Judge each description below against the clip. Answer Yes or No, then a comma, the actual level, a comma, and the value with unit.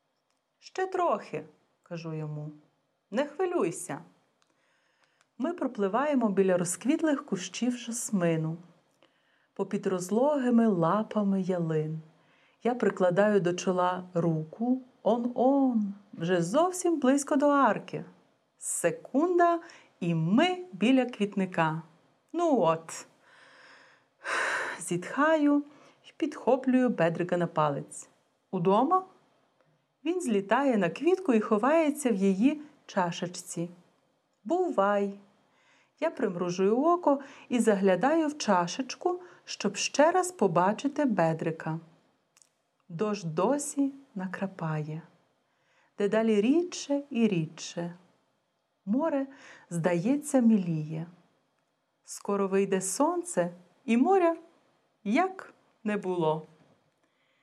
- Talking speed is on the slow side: Yes, slow, 85 wpm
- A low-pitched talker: No, high, 210 Hz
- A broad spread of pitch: Yes, wide, 8.3 semitones